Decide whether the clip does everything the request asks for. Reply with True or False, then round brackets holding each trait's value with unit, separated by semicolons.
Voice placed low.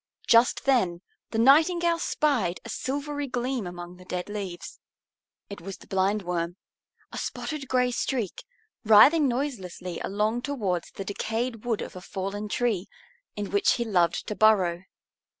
False (215 Hz)